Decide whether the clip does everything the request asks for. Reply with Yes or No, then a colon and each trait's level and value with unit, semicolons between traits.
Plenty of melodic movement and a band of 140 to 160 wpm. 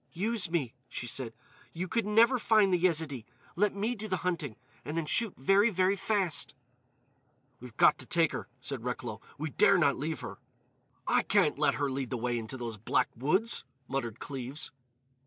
No: wide, 7.1 semitones; average, 180 wpm